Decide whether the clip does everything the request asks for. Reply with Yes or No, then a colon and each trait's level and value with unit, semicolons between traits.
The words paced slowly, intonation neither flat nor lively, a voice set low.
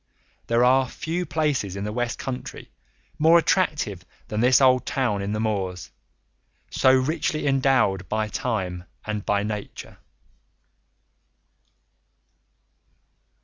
Yes: slow, 110 wpm; average, 4.7 semitones; low, 120 Hz